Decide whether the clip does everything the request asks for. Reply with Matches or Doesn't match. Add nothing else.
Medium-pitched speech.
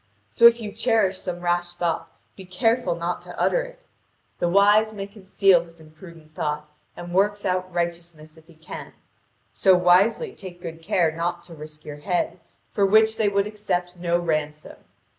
Matches